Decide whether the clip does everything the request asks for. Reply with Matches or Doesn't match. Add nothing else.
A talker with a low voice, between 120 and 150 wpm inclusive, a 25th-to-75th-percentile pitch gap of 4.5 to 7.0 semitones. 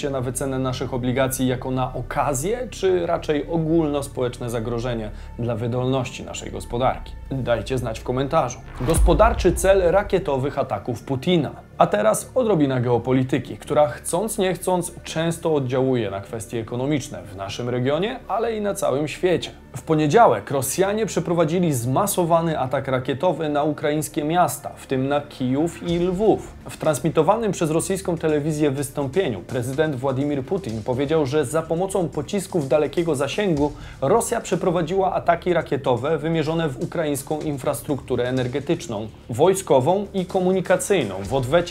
Doesn't match